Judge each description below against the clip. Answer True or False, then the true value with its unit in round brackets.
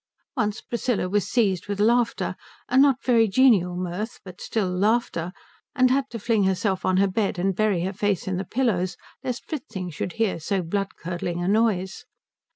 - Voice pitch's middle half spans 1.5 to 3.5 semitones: False (4.0 semitones)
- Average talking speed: True (180 wpm)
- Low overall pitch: False (200 Hz)